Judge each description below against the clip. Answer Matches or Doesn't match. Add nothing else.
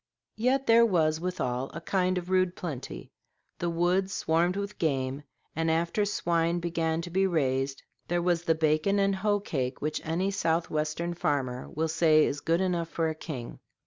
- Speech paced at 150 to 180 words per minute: Matches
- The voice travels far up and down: Doesn't match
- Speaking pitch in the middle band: Matches